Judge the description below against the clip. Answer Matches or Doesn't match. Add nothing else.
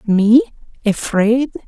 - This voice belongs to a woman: Matches